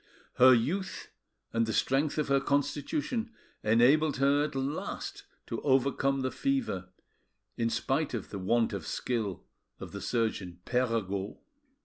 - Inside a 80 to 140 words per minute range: Yes, slow, 135 wpm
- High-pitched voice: No, low, 130 Hz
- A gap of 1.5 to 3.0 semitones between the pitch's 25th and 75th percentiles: No, average, 4.1 semitones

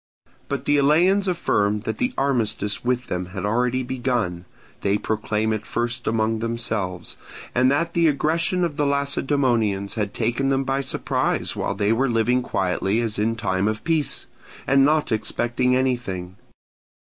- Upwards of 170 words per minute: No, average, 155 wpm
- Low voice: Yes, low, 120 Hz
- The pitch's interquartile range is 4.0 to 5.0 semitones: Yes, average, 4.5 semitones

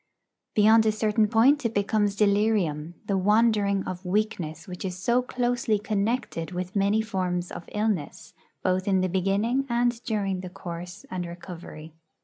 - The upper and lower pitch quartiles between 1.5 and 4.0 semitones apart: Yes, average, 3.3 semitones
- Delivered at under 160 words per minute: Yes, average, 150 wpm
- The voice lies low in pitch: No, high, 200 Hz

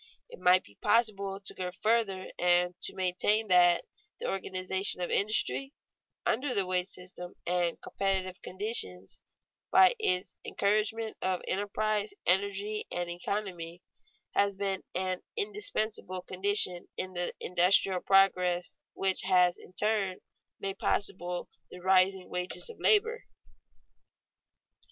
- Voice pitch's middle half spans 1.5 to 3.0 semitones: Yes, narrow, 2.4 semitones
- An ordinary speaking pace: No, slow, 120 wpm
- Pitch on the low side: No, high, 190 Hz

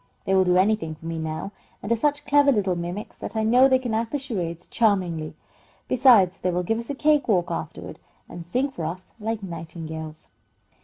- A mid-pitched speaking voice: No, high, 195 Hz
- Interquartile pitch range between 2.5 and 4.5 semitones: No, wide, 5.6 semitones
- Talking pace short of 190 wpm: No, fast, 205 wpm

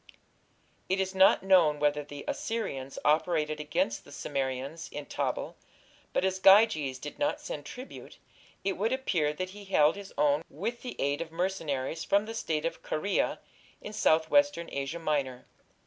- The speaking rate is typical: Yes, average, 160 wpm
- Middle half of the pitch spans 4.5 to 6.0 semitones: Yes, average, 4.9 semitones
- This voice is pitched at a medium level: Yes, medium, 160 Hz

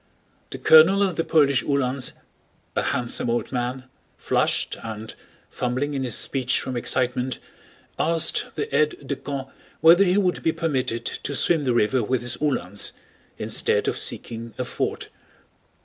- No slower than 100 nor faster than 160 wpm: Yes, average, 150 wpm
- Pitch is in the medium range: No, low, 130 Hz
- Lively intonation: No, average, 3.8 semitones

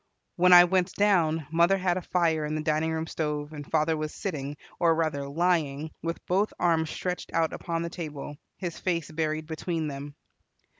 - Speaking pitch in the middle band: Yes, medium, 160 Hz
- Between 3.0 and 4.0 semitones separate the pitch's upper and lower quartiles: No, narrow, 2.4 semitones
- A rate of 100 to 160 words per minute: No, average, 185 wpm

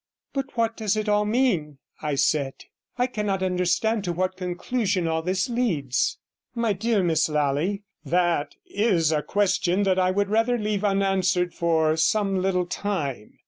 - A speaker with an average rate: Yes, average, 160 wpm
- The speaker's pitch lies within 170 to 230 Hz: Yes, medium, 185 Hz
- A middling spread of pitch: Yes, average, 3.9 semitones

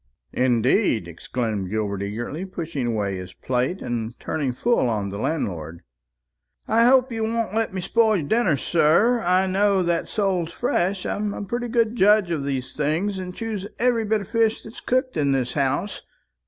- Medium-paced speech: Yes, average, 175 wpm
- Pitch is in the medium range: Yes, medium, 175 Hz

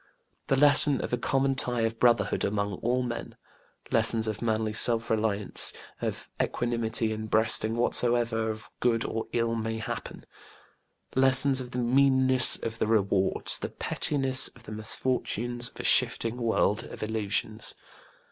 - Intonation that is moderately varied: No, narrow, 2.2 semitones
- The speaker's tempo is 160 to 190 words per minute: No, average, 145 wpm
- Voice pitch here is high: No, low, 115 Hz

